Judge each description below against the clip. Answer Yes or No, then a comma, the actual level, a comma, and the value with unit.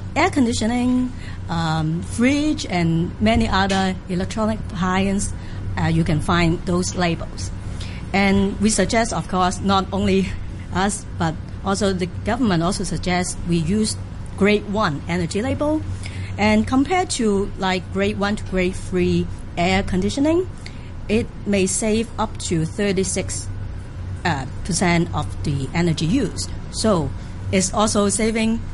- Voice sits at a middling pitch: Yes, medium, 170 Hz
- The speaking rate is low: Yes, slow, 125 wpm